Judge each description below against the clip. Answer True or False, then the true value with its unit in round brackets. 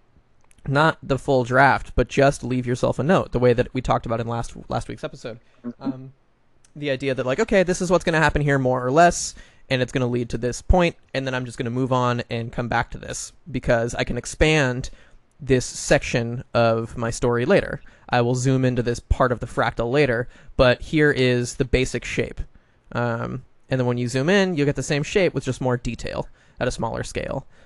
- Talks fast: True (225 wpm)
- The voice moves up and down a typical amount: False (2.2 semitones)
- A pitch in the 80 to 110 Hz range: False (125 Hz)